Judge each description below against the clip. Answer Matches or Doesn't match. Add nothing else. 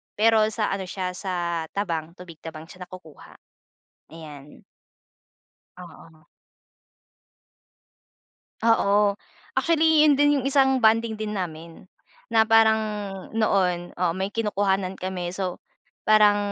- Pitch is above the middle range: Matches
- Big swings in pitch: Doesn't match